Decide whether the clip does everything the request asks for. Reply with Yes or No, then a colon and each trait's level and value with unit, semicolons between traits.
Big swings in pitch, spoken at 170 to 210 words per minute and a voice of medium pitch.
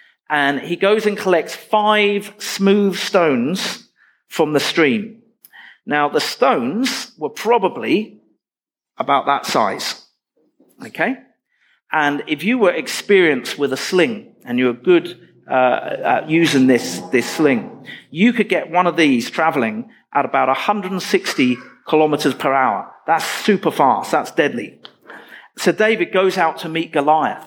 No: wide, 6.5 semitones; average, 140 wpm; medium, 180 Hz